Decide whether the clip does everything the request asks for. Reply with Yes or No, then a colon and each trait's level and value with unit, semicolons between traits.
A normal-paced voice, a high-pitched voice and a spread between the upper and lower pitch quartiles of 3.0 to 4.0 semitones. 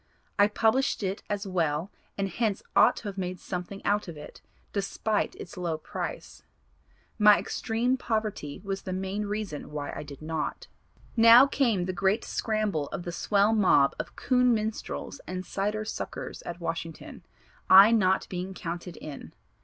Yes: average, 160 wpm; high, 195 Hz; average, 3.5 semitones